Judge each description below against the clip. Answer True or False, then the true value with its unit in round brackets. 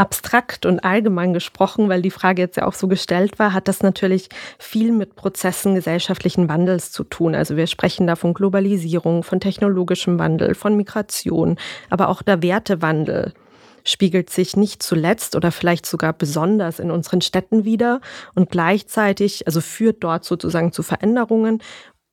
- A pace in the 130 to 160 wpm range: True (155 wpm)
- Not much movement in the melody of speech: False (3.0 semitones)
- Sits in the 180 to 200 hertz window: True (185 Hz)